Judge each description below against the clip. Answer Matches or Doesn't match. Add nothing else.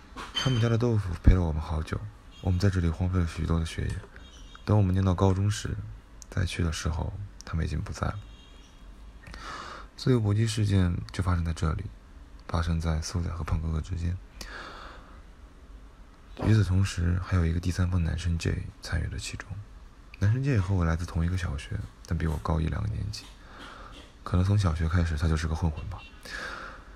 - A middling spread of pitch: Matches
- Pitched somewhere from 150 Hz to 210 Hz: Doesn't match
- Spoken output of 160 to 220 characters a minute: Doesn't match